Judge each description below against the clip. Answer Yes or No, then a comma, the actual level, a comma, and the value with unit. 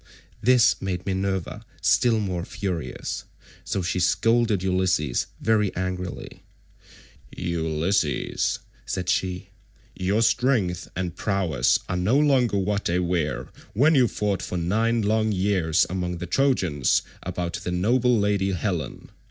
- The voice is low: Yes, very low, 95 Hz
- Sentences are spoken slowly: Yes, slow, 125 wpm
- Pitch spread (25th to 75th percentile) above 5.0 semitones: No, average, 3.6 semitones